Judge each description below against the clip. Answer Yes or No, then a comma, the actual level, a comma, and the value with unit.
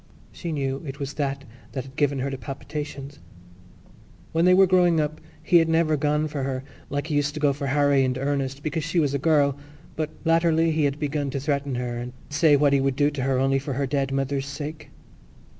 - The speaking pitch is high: No, medium, 145 Hz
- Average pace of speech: No, fast, 225 wpm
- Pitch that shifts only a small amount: Yes, narrow, 2.1 semitones